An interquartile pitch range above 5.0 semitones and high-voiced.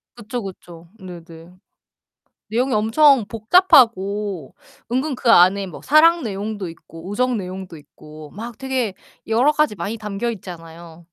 Yes: wide, 5.6 semitones; high, 205 Hz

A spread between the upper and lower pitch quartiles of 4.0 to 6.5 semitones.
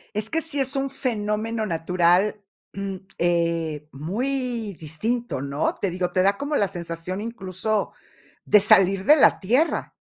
Yes: average, 5.1 semitones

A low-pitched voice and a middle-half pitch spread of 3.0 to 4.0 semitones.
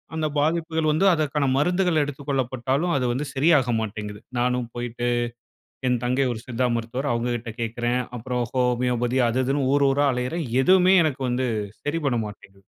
Yes: low, 130 Hz; average, 3.4 semitones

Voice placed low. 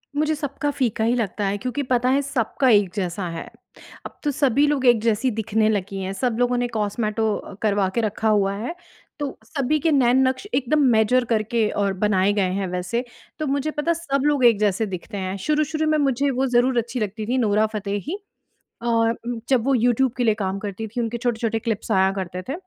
No: high, 230 Hz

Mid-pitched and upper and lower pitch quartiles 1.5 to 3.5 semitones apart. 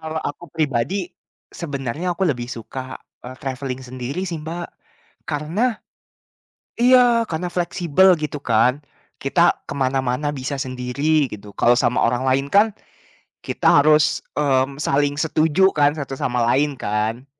No: medium, 145 Hz; average, 4.3 semitones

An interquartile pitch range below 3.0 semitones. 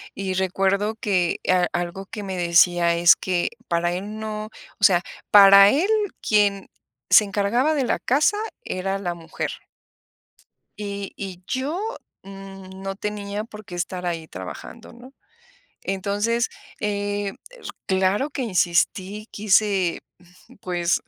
Yes: narrow, 2.6 semitones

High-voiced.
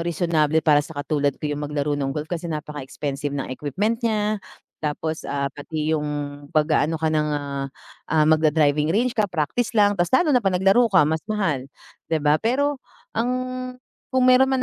No: medium, 160 Hz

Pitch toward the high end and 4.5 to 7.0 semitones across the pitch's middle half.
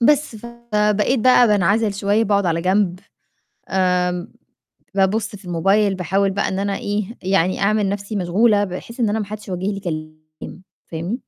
No: high, 200 Hz; average, 2.7 semitones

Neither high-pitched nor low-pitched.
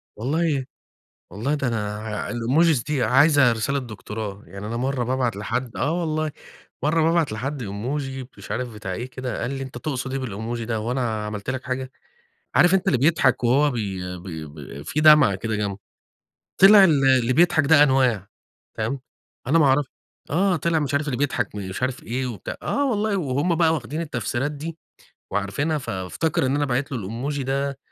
No: low, 130 Hz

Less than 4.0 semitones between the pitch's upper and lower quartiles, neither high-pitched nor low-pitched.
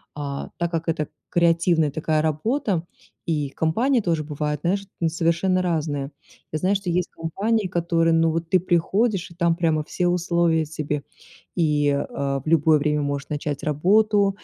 Yes: average, 2.9 semitones; medium, 165 Hz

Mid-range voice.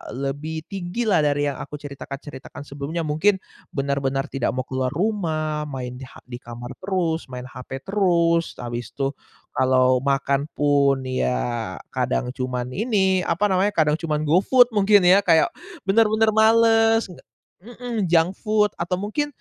Yes: medium, 155 Hz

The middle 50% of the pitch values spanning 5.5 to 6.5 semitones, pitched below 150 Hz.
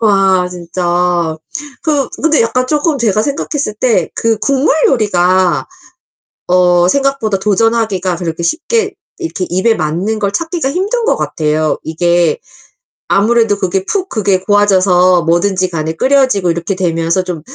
No: wide, 6.2 semitones; high, 195 Hz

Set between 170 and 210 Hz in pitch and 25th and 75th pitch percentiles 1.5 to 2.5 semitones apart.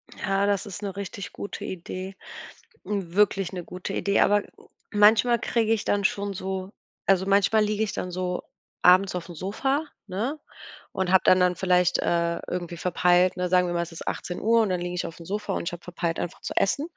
Yes: high, 190 Hz; narrow, 2.2 semitones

